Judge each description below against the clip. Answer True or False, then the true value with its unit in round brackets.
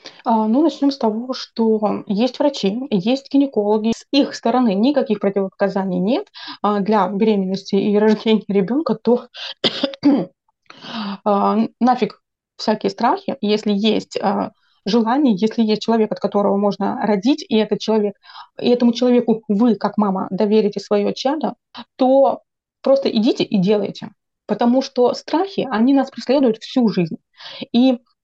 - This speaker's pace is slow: False (125 wpm)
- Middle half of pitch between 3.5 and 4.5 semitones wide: True (3.9 semitones)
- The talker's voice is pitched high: True (225 Hz)